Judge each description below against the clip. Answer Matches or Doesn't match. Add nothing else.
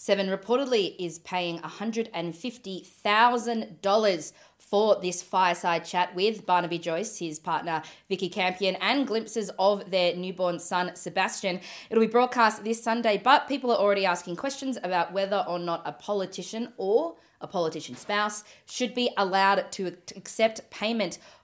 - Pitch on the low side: Doesn't match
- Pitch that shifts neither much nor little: Matches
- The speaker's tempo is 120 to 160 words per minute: Matches